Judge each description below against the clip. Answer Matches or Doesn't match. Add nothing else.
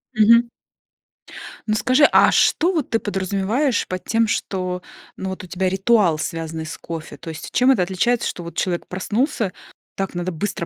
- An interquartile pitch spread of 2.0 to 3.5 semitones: Doesn't match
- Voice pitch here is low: Doesn't match